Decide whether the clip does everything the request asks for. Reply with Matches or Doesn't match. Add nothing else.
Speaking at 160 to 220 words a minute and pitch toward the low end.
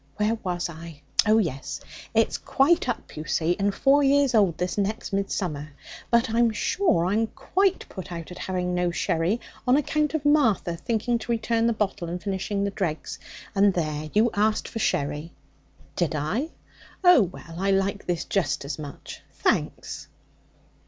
Doesn't match